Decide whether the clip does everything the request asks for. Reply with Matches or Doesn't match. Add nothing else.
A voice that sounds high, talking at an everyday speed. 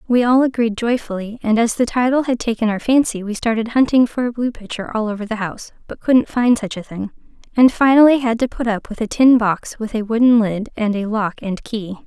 Doesn't match